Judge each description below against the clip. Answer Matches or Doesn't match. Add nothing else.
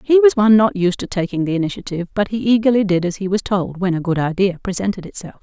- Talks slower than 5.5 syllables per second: Doesn't match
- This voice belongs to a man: Doesn't match